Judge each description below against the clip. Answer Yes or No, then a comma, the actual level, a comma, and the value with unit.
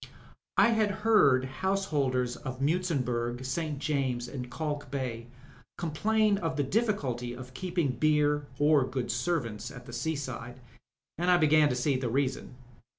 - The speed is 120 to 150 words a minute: Yes, average, 145 wpm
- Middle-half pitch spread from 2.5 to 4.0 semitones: No, average, 4.4 semitones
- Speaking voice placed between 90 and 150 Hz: Yes, medium, 140 Hz